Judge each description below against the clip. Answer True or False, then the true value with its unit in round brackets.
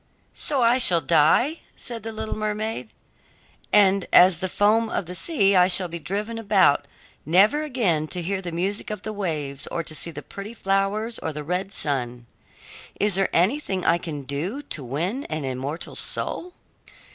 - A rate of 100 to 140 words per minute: False (175 wpm)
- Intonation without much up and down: False (5.2 semitones)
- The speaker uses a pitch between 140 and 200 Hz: True (190 Hz)